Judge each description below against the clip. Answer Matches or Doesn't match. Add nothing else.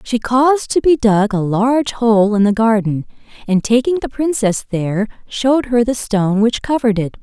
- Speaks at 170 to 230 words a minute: Matches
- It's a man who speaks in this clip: Doesn't match